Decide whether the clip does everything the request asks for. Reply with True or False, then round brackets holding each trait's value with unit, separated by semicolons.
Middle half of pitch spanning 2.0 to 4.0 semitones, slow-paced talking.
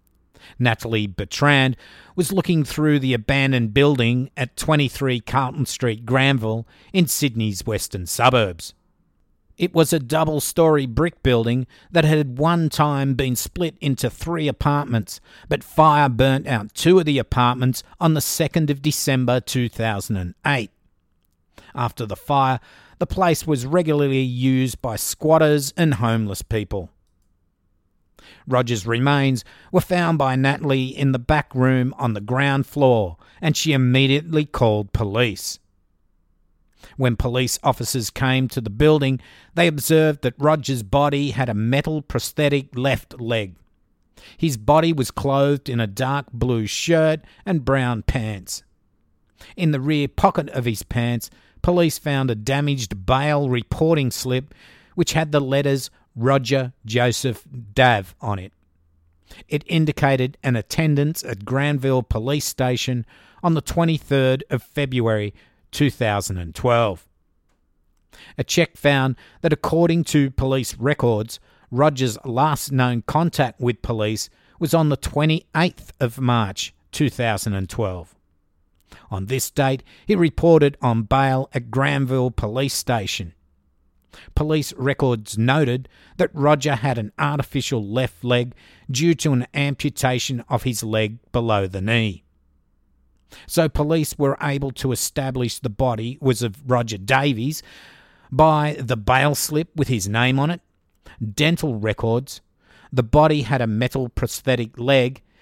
False (4.6 semitones; 130 wpm)